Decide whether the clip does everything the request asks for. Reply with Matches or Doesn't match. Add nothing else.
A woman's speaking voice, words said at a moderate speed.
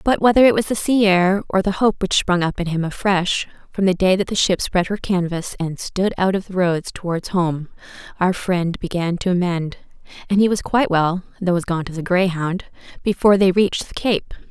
Doesn't match